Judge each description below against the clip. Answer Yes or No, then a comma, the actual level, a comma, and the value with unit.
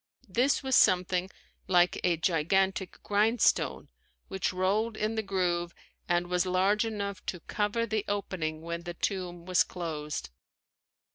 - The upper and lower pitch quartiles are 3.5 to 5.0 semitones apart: No, average, 2.9 semitones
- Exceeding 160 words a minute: No, slow, 135 wpm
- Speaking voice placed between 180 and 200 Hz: Yes, medium, 185 Hz